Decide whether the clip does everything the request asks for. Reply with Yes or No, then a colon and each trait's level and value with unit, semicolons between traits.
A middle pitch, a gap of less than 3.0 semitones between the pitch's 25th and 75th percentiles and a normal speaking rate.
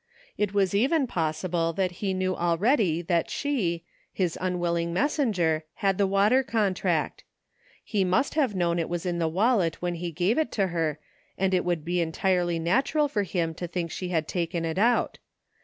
No: medium, 180 Hz; average, 3.3 semitones; average, 180 wpm